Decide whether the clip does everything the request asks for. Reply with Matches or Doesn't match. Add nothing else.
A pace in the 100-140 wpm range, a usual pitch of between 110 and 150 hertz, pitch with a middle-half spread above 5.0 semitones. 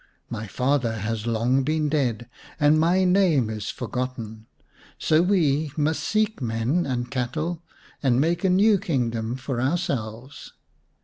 Matches